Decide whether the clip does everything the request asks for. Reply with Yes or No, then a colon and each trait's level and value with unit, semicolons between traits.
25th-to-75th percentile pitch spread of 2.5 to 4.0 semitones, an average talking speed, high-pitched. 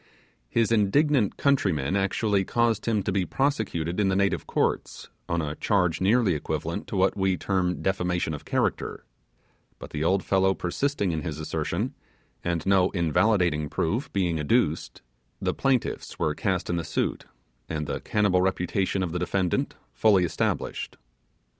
No: average, 3.3 semitones; average, 155 wpm; very low, 95 Hz